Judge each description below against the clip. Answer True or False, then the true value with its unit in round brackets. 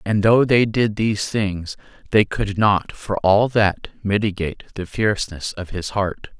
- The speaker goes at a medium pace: True (170 wpm)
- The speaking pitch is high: False (100 Hz)